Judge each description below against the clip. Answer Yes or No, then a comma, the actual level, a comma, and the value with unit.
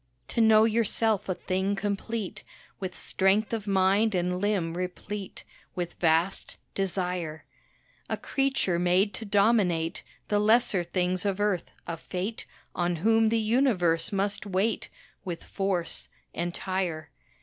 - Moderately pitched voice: No, high, 195 Hz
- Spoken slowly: Yes, slow, 125 wpm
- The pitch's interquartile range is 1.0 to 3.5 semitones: Yes, average, 3.1 semitones